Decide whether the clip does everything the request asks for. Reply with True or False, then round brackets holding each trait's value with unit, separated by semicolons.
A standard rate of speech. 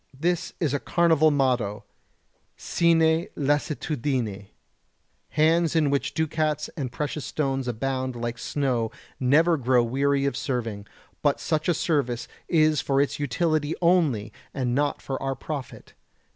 False (130 wpm)